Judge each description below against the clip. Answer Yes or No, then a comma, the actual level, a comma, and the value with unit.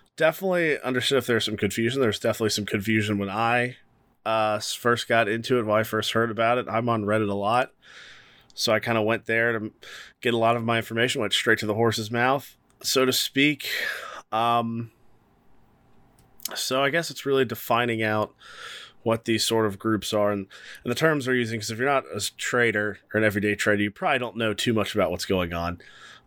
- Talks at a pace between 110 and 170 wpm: No, fast, 205 wpm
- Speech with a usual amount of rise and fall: No, narrow, 2.3 semitones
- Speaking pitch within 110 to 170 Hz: Yes, low, 115 Hz